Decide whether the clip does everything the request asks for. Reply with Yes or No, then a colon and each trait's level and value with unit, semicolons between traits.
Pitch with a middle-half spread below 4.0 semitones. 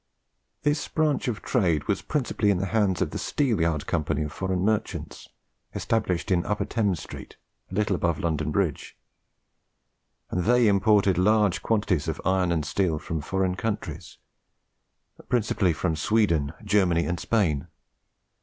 No: average, 4.3 semitones